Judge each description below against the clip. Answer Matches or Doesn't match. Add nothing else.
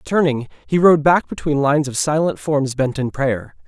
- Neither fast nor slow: Matches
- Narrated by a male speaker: Matches